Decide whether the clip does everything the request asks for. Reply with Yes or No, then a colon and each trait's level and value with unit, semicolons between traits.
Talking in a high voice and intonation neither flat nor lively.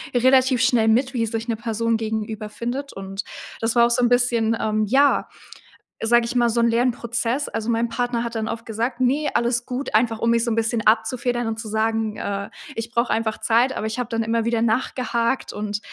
No: high, 230 Hz; narrow, 1.5 semitones